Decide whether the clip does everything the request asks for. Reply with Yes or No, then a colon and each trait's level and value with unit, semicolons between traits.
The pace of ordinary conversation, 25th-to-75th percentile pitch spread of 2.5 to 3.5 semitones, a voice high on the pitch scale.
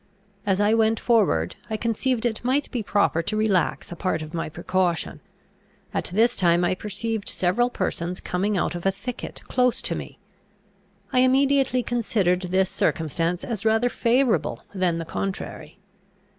No: average, 155 wpm; average, 4.8 semitones; high, 205 Hz